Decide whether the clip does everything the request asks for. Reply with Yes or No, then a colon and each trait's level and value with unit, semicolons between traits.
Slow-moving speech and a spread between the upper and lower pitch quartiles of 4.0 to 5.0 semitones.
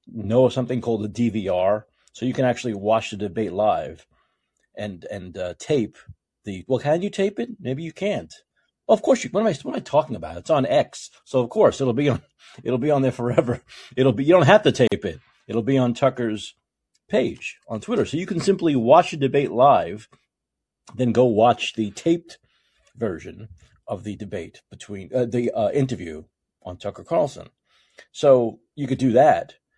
No: average, 195 wpm; average, 4.4 semitones